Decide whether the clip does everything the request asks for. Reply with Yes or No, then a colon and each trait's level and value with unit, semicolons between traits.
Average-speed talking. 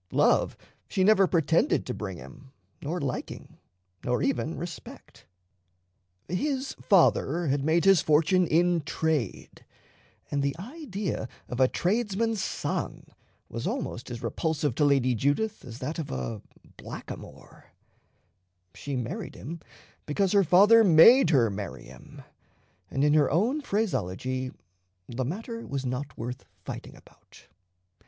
No: slow, 130 wpm